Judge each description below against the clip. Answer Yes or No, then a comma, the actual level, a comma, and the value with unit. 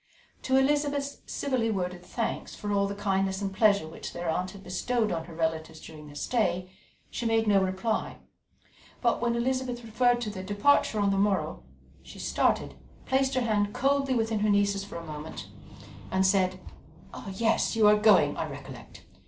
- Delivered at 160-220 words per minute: Yes, average, 175 wpm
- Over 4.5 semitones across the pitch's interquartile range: No, average, 4.1 semitones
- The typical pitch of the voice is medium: No, high, 205 Hz